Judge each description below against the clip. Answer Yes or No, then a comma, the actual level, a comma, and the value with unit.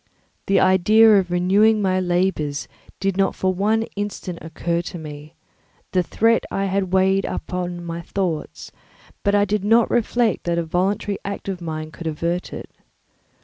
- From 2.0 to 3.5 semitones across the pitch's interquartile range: Yes, average, 2.8 semitones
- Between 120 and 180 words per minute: Yes, average, 165 wpm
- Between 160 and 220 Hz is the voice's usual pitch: Yes, medium, 185 Hz